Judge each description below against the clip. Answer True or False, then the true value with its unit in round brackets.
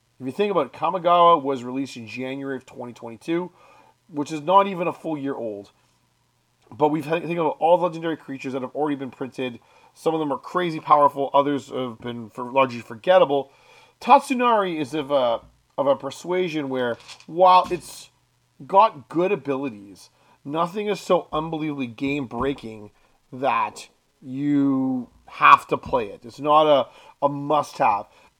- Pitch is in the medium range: True (145 Hz)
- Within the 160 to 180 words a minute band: True (165 wpm)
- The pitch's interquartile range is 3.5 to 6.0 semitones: True (4.6 semitones)